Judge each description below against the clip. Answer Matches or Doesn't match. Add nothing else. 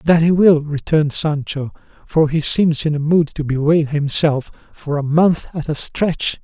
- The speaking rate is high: Doesn't match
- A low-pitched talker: Doesn't match